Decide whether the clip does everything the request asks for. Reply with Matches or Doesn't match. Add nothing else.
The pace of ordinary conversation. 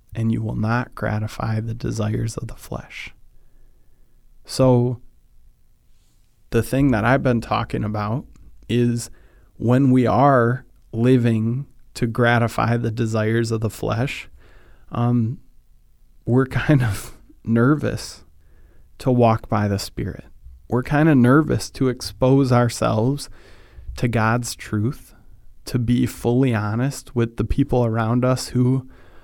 Doesn't match